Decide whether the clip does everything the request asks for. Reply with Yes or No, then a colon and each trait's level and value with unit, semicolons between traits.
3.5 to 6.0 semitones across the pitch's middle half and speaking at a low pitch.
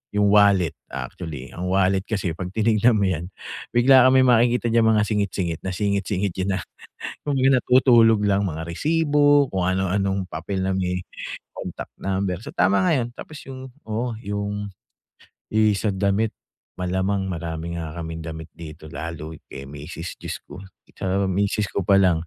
Yes: average, 3.9 semitones; very low, 95 Hz